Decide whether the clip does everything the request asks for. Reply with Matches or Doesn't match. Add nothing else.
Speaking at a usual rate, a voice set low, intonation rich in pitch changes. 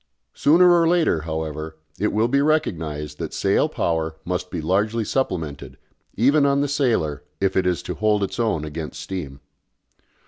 Matches